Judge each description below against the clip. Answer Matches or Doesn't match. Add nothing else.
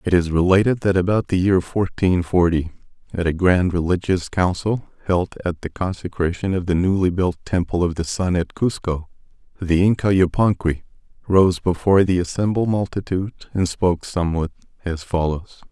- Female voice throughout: Doesn't match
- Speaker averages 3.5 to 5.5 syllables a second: Matches